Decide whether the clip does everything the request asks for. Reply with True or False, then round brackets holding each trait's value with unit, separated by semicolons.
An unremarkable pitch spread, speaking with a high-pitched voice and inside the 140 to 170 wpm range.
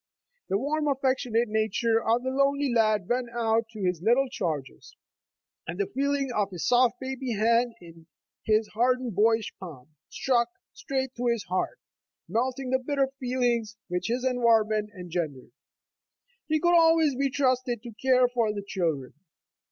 True (3.7 semitones; 235 Hz; 150 wpm)